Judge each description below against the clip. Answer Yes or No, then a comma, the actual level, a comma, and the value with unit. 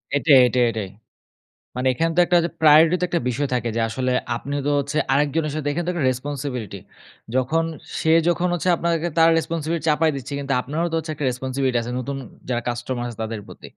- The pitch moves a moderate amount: Yes, average, 4.4 semitones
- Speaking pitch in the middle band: Yes, medium, 145 Hz